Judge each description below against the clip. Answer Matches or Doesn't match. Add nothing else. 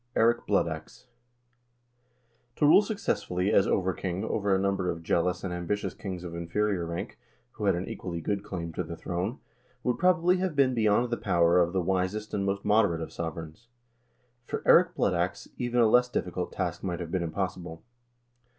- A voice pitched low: Matches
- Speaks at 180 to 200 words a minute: Matches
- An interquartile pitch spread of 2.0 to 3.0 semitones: Doesn't match